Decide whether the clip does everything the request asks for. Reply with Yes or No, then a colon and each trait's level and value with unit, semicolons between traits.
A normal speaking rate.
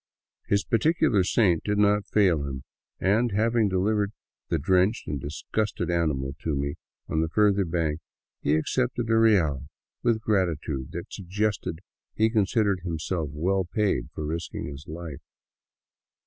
Yes: average, 150 wpm